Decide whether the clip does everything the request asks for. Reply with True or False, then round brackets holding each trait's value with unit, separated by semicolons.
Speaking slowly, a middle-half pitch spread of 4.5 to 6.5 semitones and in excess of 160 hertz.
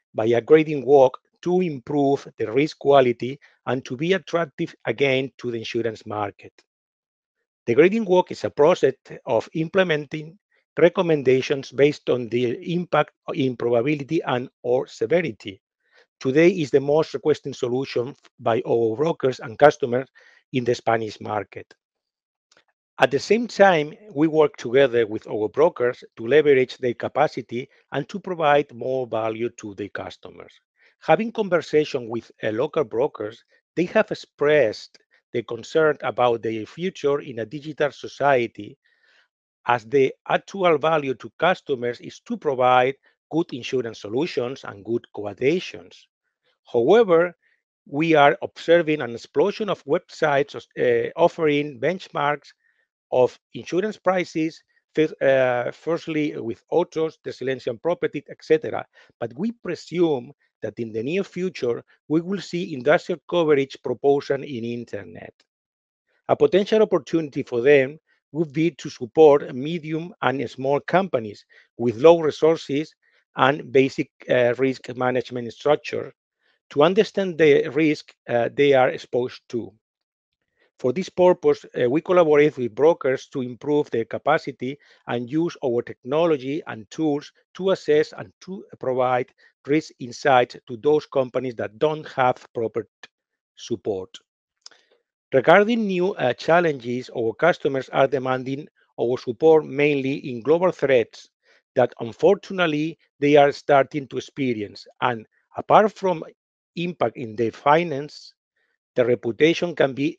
False (130 wpm; 5.2 semitones; 145 Hz)